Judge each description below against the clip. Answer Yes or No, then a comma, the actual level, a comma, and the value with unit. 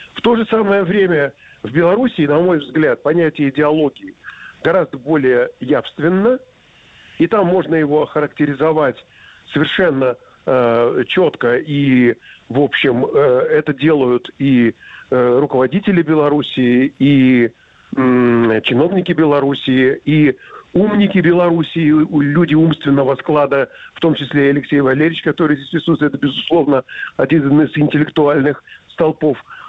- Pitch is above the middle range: No, medium, 150 Hz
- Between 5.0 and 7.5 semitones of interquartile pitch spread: No, average, 3.5 semitones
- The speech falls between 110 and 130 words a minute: Yes, average, 115 wpm